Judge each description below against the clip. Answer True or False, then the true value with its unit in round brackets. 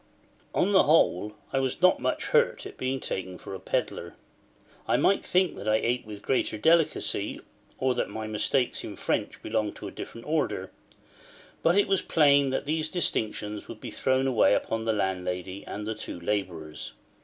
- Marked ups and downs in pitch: True (6.3 semitones)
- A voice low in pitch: True (115 Hz)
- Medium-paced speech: True (180 wpm)